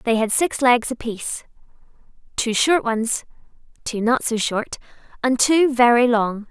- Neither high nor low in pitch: No, high, 240 Hz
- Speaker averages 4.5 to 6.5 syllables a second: No, 4.2 syllables/s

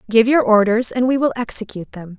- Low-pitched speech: No, high, 225 Hz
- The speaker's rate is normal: No, fast, 220 wpm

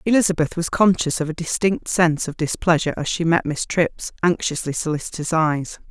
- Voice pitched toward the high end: No, medium, 165 Hz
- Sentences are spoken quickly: No, average, 175 wpm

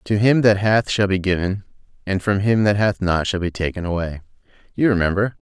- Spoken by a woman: No, male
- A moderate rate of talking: No, fast, 210 wpm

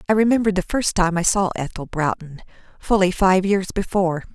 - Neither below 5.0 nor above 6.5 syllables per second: Yes, 5.8 syllables/s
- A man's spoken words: No, female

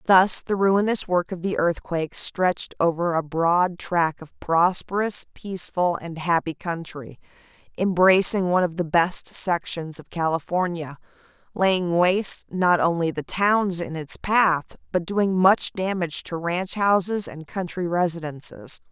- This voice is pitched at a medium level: Yes, medium, 175 Hz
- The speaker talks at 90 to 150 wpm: Yes, average, 145 wpm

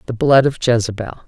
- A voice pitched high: No, low, 135 Hz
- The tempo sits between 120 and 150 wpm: No, average, 190 wpm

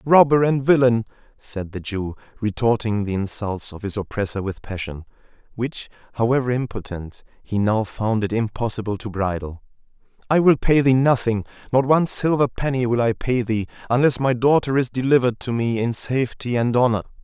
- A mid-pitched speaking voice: No, low, 115 Hz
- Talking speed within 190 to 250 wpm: No, average, 165 wpm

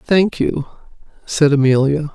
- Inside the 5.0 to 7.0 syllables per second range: No, 4.1 syllables/s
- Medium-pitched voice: Yes, medium, 150 Hz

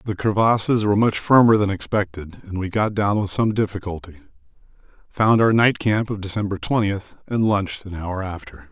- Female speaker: No, male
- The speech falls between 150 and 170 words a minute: No, average, 180 wpm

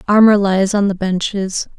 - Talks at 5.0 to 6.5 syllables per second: No, 4.5 syllables/s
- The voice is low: No, high, 195 Hz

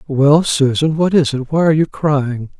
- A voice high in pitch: No, medium, 145 Hz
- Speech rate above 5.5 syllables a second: No, 4.6 syllables/s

